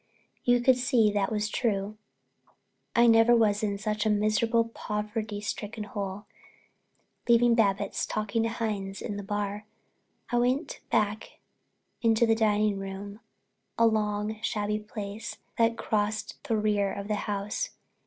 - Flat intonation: Yes, narrow, 1.7 semitones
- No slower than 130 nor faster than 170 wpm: Yes, average, 140 wpm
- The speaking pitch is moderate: No, high, 215 Hz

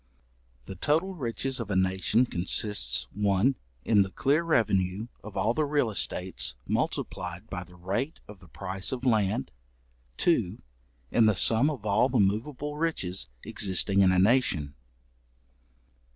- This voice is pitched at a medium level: No, low, 105 Hz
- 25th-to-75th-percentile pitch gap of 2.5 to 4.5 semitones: No, wide, 5.5 semitones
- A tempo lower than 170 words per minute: Yes, average, 145 wpm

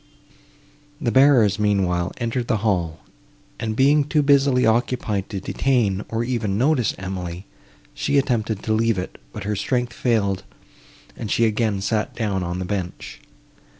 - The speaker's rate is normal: Yes, average, 150 wpm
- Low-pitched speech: Yes, low, 110 Hz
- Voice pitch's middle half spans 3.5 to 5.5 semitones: Yes, average, 4.1 semitones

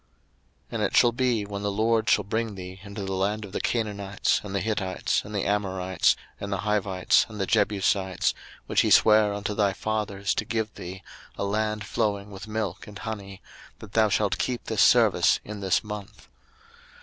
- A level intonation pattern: Yes, narrow, 1.8 semitones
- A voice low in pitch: Yes, low, 105 Hz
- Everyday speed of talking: Yes, average, 190 wpm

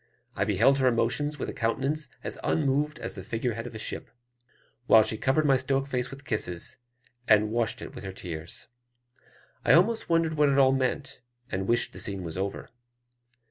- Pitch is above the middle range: No, low, 125 Hz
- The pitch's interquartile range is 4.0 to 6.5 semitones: Yes, average, 4.5 semitones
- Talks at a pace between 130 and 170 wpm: No, average, 190 wpm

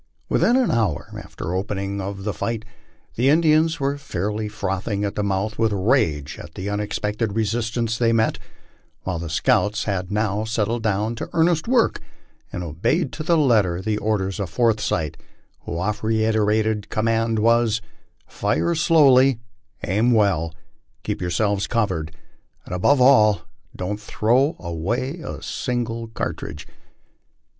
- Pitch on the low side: Yes, low, 110 Hz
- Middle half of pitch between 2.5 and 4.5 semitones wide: Yes, average, 3.3 semitones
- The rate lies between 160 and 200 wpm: No, average, 145 wpm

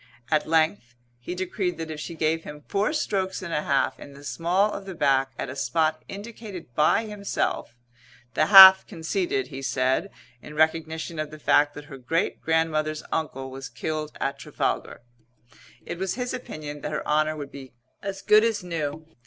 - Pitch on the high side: No, medium, 160 Hz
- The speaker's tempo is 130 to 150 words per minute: No, average, 180 wpm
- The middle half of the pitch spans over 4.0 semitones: Yes, average, 4.4 semitones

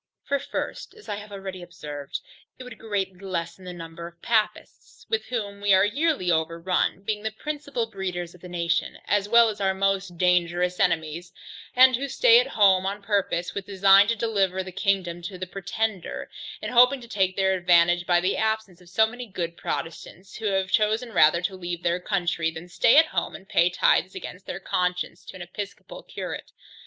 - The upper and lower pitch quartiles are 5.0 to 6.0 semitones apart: No, average, 3.4 semitones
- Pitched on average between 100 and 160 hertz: No, high, 190 Hz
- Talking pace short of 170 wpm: No, average, 195 wpm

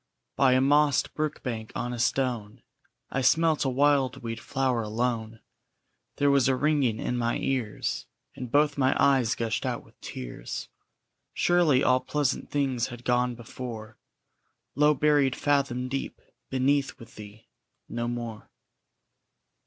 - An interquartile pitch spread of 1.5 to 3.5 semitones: Yes, average, 3.2 semitones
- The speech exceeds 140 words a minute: No, slow, 135 wpm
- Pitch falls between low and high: No, low, 130 Hz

